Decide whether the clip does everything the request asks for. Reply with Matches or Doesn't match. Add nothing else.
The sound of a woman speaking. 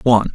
Doesn't match